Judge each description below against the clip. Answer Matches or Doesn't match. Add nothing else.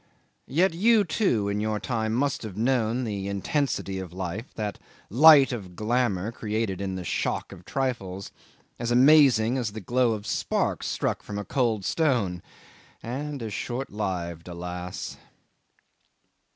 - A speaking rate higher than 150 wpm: Doesn't match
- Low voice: Matches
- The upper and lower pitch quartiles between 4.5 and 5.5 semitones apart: Matches